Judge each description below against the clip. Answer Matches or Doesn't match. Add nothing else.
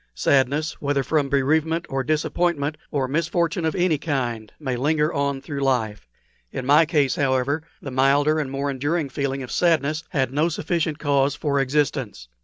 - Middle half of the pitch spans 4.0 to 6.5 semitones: Doesn't match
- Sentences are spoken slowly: Doesn't match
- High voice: Doesn't match